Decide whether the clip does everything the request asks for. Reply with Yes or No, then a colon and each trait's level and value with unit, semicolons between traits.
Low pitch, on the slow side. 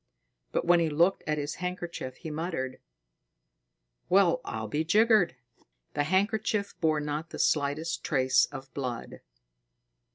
No: medium, 160 Hz; slow, 130 wpm